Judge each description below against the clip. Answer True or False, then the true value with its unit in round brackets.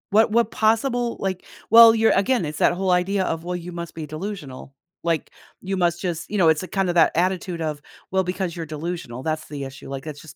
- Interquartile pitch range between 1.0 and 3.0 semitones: False (3.7 semitones)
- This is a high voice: False (175 Hz)